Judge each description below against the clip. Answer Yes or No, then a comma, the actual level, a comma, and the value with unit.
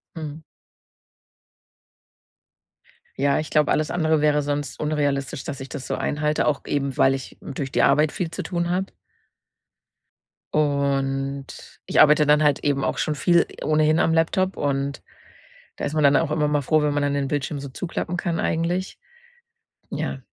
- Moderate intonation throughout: No, narrow, 1.9 semitones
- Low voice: No, medium, 150 Hz